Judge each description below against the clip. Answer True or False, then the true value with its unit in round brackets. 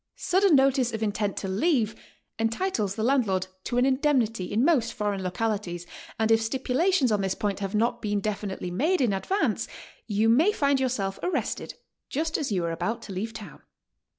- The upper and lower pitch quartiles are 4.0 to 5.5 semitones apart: True (4.9 semitones)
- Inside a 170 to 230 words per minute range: True (180 wpm)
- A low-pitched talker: False (225 Hz)